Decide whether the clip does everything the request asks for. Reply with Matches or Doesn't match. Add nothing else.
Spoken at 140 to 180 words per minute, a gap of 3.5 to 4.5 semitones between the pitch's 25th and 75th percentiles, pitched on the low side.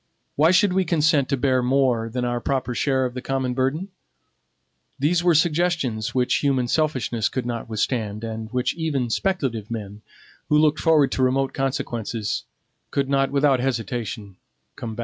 Matches